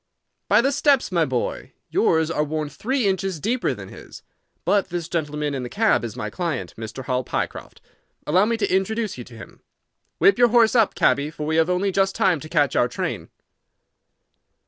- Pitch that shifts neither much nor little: No, wide, 5.9 semitones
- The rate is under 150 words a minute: No, average, 190 wpm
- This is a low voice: No, medium, 170 Hz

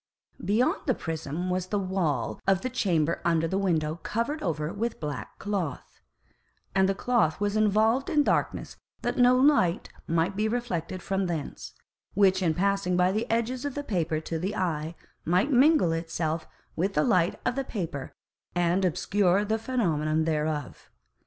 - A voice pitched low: No, medium, 185 Hz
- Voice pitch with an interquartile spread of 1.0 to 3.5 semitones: No, average, 4.9 semitones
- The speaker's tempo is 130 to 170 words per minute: Yes, average, 165 wpm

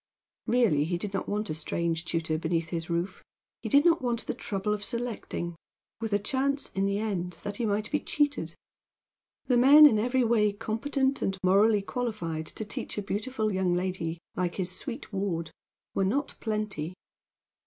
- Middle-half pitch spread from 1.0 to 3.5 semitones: No, average, 5.1 semitones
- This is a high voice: Yes, high, 205 Hz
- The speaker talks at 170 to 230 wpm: Yes, average, 175 wpm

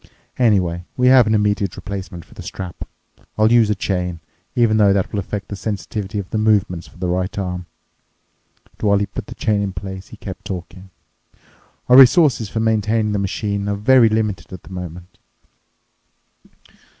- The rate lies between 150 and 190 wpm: Yes, average, 175 wpm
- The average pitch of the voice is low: Yes, low, 100 Hz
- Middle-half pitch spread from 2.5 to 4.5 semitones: Yes, average, 2.9 semitones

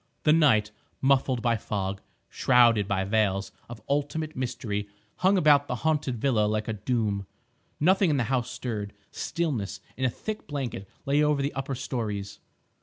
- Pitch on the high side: No, low, 125 Hz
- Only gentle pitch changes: No, average, 5.2 semitones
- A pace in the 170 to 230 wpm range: No, average, 160 wpm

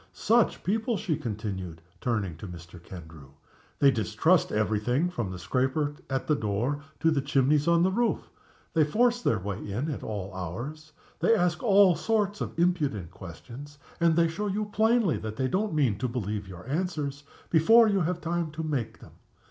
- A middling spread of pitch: No, wide, 8.9 semitones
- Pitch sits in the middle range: Yes, medium, 145 Hz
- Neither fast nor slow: Yes, average, 180 wpm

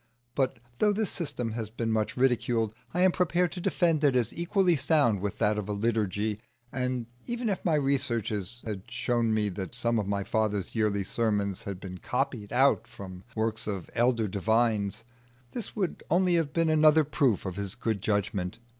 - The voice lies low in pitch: Yes, low, 115 Hz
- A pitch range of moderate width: No, wide, 5.8 semitones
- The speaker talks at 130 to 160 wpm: No, average, 185 wpm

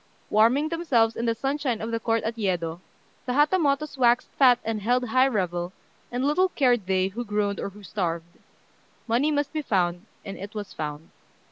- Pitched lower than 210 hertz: No, high, 225 Hz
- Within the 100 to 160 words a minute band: No, average, 180 wpm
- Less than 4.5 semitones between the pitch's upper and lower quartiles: No, wide, 5.5 semitones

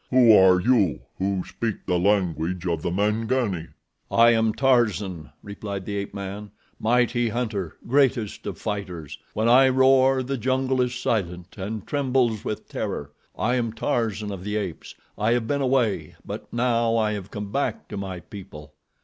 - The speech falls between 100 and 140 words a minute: No, average, 165 wpm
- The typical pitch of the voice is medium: No, low, 110 Hz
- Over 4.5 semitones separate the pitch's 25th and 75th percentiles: No, average, 4.2 semitones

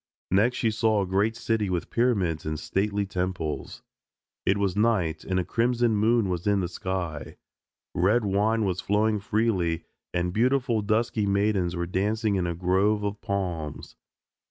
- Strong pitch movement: No, average, 3.3 semitones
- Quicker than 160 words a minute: No, average, 155 wpm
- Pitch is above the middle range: No, low, 100 Hz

